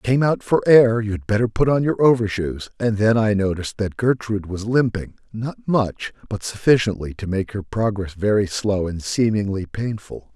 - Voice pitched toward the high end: No, low, 110 Hz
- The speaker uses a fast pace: No, average, 185 wpm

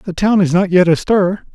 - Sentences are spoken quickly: Yes, fast, 230 wpm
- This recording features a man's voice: Yes, male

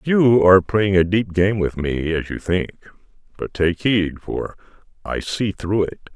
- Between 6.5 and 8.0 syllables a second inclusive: No, 4.0 syllables/s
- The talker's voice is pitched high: No, very low, 95 Hz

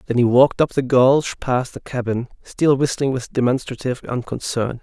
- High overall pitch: No, low, 125 Hz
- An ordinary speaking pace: Yes, average, 175 wpm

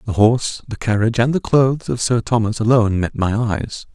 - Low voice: Yes, low, 115 Hz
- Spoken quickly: Yes, fast, 215 wpm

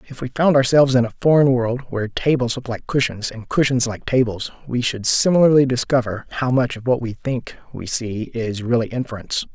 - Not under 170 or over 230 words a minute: Yes, average, 200 wpm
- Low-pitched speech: Yes, low, 125 Hz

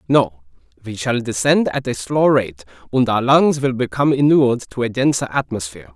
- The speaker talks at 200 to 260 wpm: No, average, 180 wpm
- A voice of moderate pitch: No, low, 120 Hz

